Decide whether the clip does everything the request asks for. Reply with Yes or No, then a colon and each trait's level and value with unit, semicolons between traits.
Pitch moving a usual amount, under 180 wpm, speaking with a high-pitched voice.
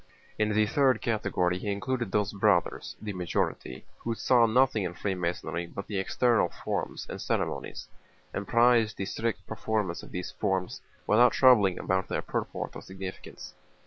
No: average, 3.6 semitones; average, 155 wpm; low, 105 Hz